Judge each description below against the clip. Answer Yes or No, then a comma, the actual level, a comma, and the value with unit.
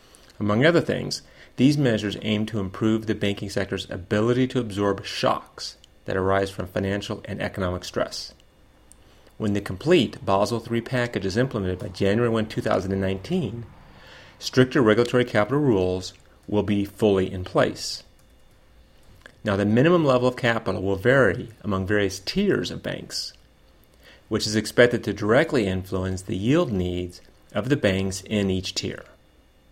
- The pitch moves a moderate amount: Yes, average, 3.3 semitones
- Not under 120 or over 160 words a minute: Yes, average, 145 wpm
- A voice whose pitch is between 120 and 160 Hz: No, low, 100 Hz